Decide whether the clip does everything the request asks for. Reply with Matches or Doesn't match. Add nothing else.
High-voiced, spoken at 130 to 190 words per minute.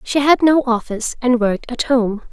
Doesn't match